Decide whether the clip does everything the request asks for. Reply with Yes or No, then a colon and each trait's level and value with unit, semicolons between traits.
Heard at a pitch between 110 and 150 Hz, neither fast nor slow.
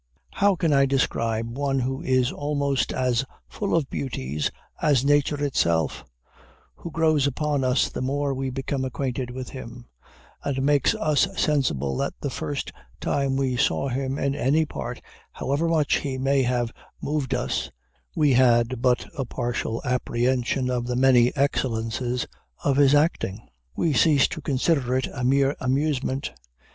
Yes: low, 135 Hz; average, 155 wpm